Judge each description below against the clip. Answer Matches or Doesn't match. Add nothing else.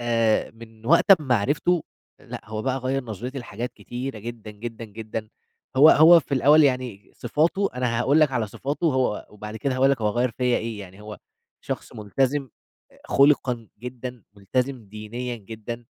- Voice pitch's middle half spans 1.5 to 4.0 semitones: Matches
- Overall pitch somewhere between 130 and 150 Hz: Doesn't match